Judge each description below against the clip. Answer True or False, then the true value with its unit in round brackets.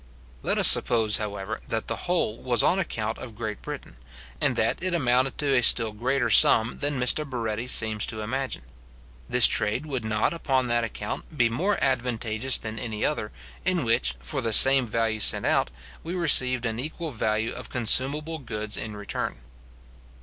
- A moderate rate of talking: True (175 wpm)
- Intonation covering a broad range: False (3.6 semitones)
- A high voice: False (120 Hz)